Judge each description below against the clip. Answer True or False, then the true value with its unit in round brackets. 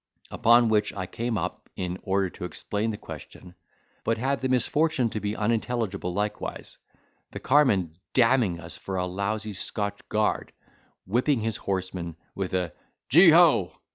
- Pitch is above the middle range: False (105 Hz)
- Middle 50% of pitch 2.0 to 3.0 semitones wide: False (4.3 semitones)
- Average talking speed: True (150 wpm)